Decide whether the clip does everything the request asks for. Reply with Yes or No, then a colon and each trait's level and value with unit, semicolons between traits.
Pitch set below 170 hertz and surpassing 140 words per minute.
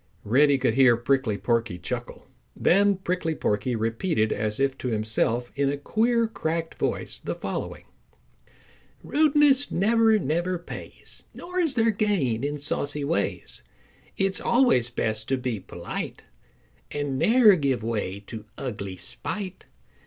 No: medium, 140 Hz; slow, 135 wpm